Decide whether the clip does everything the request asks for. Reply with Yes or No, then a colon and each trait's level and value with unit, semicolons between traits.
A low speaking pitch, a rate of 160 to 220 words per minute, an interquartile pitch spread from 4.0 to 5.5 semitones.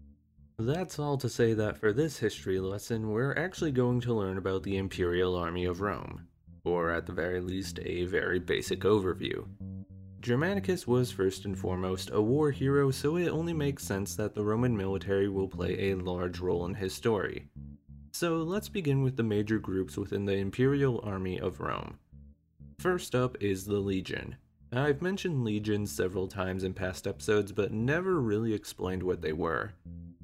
Yes: low, 100 Hz; average, 175 wpm; average, 5.2 semitones